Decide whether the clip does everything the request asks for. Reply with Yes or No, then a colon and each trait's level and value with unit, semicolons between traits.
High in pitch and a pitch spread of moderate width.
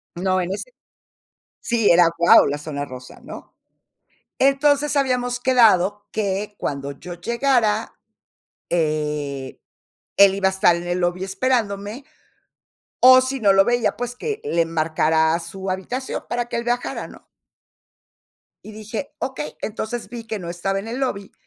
No: high, 200 Hz; wide, 5.9 semitones